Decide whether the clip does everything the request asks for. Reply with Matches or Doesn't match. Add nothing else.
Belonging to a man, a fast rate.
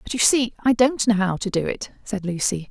Doesn't match